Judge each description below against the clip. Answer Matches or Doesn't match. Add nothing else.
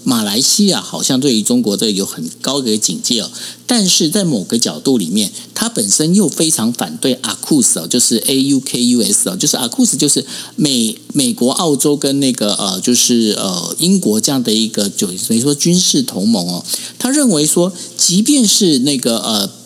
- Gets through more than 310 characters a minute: Doesn't match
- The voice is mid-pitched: Matches